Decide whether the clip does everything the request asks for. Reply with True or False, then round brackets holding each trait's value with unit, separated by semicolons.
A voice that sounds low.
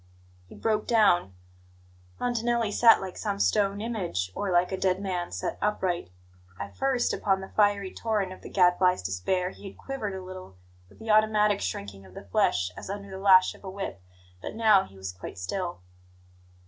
False (190 Hz)